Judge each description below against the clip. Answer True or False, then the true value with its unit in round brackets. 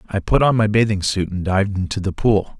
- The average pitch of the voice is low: True (100 Hz)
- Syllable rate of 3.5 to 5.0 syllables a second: False (6.0 syllables/s)